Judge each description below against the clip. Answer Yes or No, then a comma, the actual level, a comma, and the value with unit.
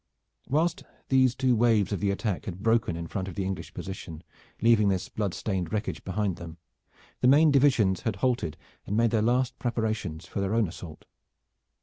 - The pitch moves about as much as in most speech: Yes, average, 4.2 semitones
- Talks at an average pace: Yes, average, 185 wpm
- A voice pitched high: No, low, 105 Hz